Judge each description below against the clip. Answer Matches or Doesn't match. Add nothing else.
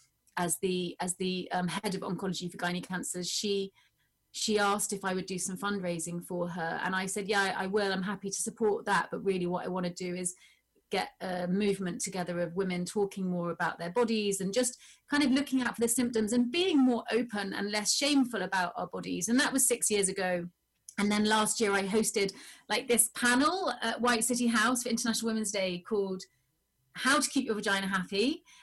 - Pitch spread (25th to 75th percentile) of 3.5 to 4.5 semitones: Matches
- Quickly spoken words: Matches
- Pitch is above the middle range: Matches